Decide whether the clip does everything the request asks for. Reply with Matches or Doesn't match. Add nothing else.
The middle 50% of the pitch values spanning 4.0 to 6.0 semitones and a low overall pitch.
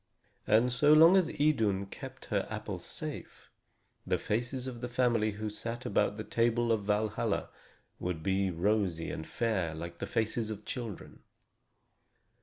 Doesn't match